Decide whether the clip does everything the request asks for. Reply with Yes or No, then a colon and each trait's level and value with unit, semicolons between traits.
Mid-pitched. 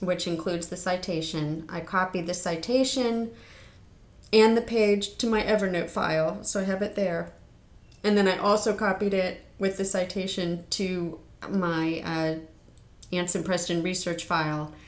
Yes: medium, 180 Hz